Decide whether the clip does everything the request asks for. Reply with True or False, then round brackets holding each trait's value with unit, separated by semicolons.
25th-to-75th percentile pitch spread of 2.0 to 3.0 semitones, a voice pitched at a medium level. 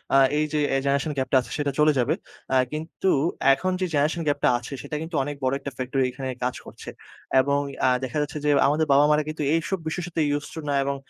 True (2.4 semitones; 145 Hz)